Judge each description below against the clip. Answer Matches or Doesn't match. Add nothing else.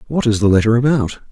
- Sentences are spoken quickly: Matches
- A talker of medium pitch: Doesn't match